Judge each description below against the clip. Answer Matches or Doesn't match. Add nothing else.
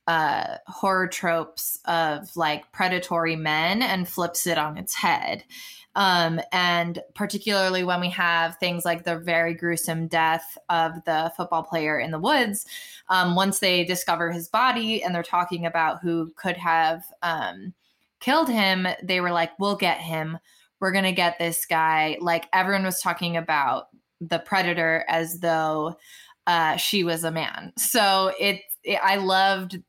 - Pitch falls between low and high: Matches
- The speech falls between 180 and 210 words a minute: Doesn't match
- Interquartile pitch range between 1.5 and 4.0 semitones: Matches